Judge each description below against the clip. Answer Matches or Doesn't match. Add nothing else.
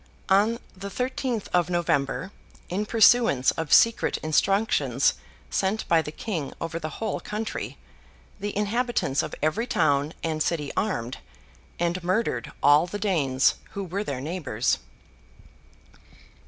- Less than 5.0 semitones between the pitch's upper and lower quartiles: Doesn't match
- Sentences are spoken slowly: Matches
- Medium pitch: Matches